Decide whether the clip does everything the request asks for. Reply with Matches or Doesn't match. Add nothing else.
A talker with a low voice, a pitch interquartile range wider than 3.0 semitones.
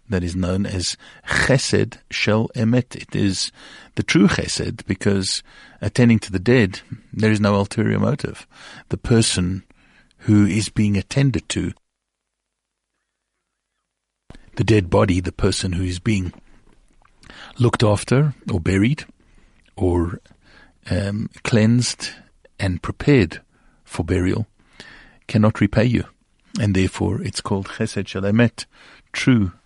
Matches